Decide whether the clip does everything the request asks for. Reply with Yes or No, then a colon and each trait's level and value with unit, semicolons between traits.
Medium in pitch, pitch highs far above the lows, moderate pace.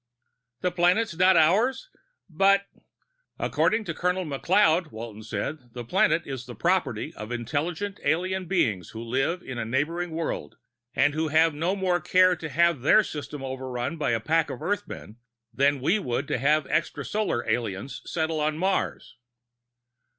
Yes: medium, 155 Hz; wide, 6.0 semitones; average, 155 wpm